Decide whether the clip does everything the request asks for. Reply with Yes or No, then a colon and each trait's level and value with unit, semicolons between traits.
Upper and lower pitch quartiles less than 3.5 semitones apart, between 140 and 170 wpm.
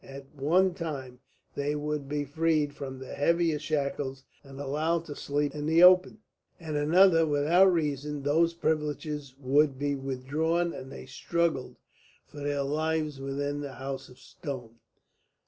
Yes: average, 2.7 semitones; average, 145 wpm